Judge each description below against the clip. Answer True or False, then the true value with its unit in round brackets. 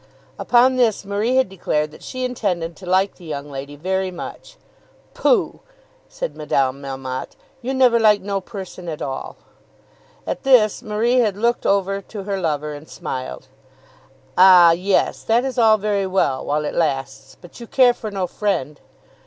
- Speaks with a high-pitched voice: True (195 Hz)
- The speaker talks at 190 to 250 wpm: False (165 wpm)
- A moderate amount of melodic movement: False (6.7 semitones)